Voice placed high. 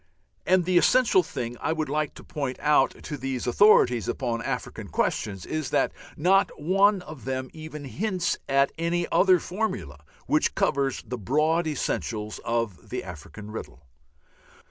No: medium, 145 Hz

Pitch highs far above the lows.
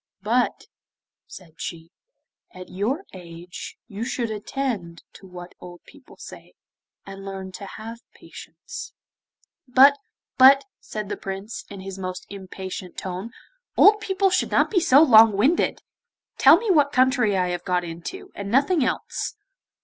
Yes: wide, 6.7 semitones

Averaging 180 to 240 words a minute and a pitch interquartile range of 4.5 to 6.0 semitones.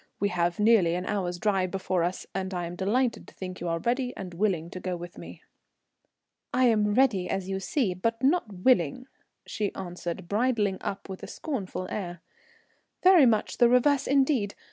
Yes: average, 190 wpm; average, 5.0 semitones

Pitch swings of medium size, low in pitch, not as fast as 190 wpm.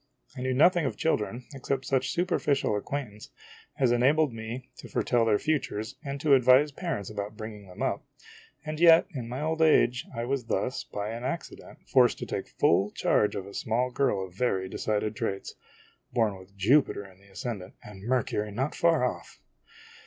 Yes: average, 4.9 semitones; low, 120 Hz; average, 180 wpm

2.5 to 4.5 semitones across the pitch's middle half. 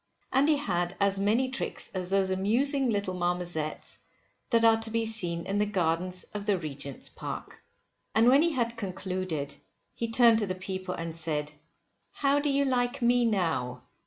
No: average, 5.0 semitones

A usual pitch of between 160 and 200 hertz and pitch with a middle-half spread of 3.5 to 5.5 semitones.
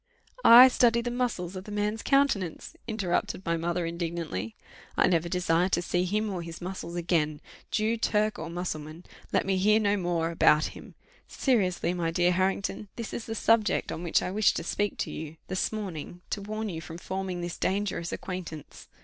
Yes: medium, 185 Hz; average, 3.8 semitones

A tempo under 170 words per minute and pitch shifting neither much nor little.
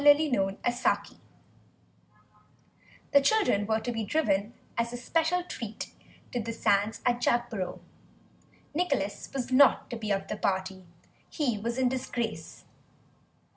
Yes: slow, 135 wpm; average, 4.8 semitones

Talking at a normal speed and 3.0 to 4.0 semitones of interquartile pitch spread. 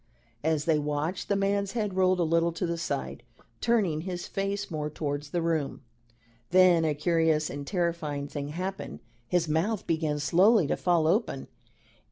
Yes: average, 165 wpm; average, 3.6 semitones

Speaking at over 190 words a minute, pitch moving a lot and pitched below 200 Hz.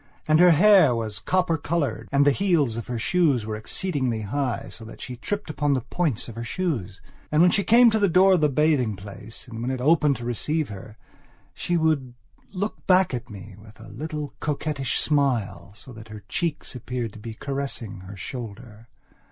Yes: average, 200 wpm; wide, 6.1 semitones; low, 135 Hz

